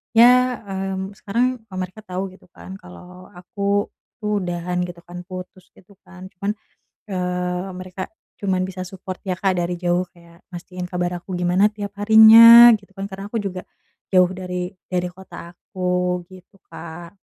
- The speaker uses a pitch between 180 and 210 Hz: Yes, medium, 185 Hz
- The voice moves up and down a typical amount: No, narrow, 1.9 semitones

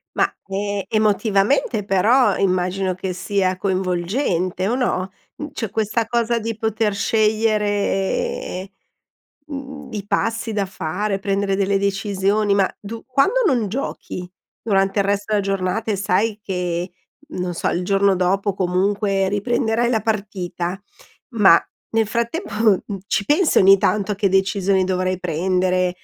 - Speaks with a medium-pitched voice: No, high, 200 Hz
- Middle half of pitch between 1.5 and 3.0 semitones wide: Yes, average, 2.7 semitones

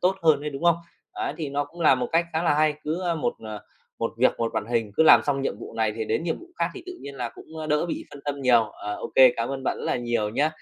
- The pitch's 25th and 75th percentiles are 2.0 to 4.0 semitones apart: No, average, 5.2 semitones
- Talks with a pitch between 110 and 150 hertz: Yes, medium, 140 Hz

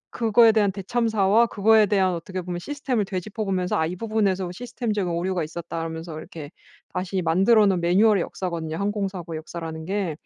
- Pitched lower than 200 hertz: Yes, high, 190 Hz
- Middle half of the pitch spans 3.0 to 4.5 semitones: Yes, average, 3.7 semitones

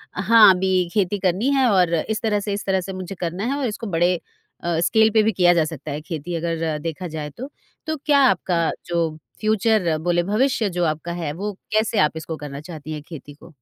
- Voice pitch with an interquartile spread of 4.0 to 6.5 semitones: Yes, average, 4.3 semitones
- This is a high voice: No, medium, 180 Hz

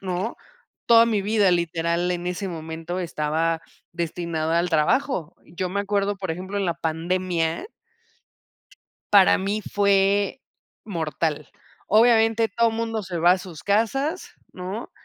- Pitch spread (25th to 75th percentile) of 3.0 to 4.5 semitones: Yes, average, 3.6 semitones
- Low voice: No, medium, 185 Hz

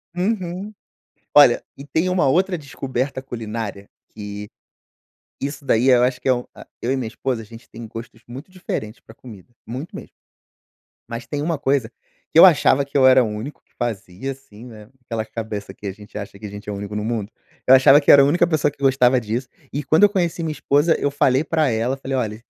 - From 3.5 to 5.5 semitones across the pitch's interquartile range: Yes, average, 4.4 semitones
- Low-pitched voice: Yes, low, 130 Hz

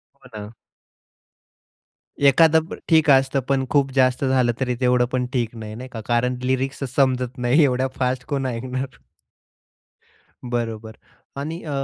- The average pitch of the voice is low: Yes, low, 130 Hz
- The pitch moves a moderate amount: No, narrow, 1.9 semitones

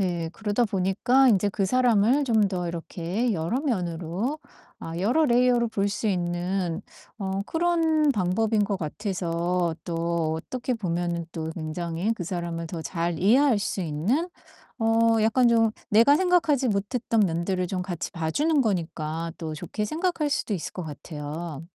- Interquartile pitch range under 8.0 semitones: Yes, wide, 5.6 semitones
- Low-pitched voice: No, high, 195 Hz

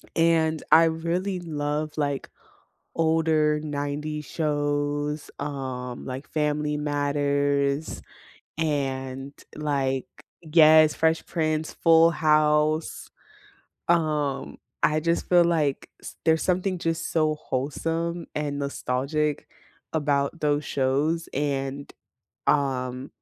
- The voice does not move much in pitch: Yes, narrow, 2.1 semitones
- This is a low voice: No, medium, 150 Hz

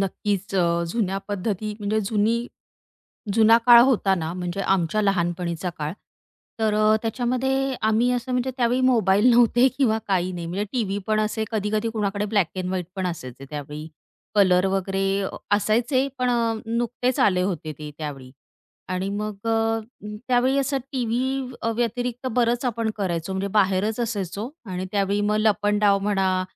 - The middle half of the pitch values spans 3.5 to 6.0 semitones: Yes, average, 3.8 semitones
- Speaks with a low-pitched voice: No, high, 210 Hz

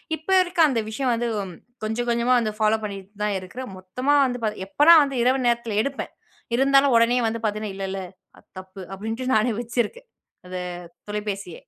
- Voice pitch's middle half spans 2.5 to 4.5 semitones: Yes, average, 3.6 semitones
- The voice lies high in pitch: Yes, high, 230 Hz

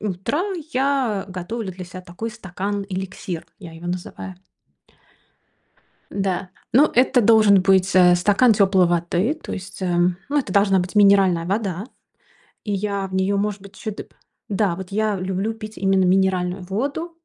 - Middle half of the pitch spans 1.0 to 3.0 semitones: Yes, narrow, 2.6 semitones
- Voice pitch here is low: No, high, 195 Hz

